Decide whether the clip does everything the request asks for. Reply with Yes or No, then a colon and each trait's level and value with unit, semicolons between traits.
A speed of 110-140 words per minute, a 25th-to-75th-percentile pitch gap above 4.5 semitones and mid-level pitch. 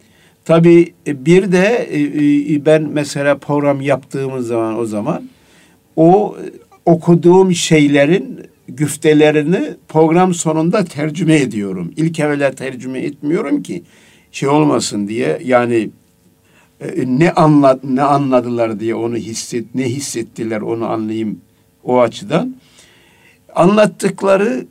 No: average, 100 wpm; average, 5.3 semitones; medium, 145 Hz